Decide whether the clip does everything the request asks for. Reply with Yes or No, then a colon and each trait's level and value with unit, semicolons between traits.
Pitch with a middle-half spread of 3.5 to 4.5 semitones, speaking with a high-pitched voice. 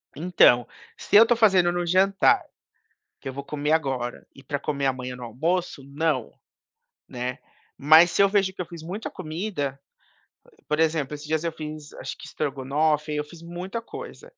No: average, 4.0 semitones; medium, 155 Hz